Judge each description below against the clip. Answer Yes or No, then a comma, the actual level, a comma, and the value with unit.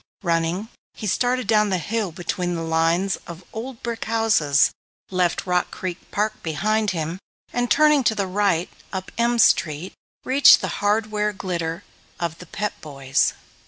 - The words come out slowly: No, average, 155 wpm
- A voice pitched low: No, high, 190 Hz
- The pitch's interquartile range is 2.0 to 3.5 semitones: No, average, 4.6 semitones